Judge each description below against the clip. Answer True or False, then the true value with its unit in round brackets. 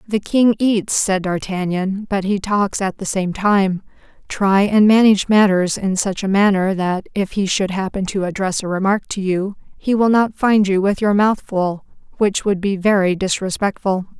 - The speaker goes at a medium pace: True (185 wpm)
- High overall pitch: True (195 Hz)